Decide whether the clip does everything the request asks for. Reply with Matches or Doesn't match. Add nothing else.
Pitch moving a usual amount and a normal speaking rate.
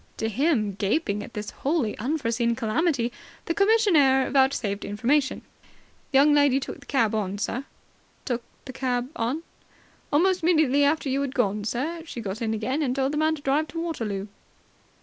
Matches